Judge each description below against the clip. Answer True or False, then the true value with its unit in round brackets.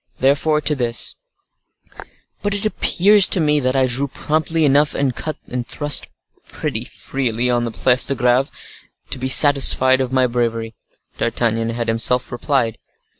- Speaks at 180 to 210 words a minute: False (155 wpm)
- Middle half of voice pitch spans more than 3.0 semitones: True (3.4 semitones)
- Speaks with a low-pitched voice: True (130 Hz)